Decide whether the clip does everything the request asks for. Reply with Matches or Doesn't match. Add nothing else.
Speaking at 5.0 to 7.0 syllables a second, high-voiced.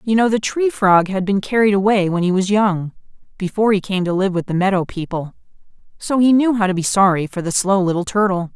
Matches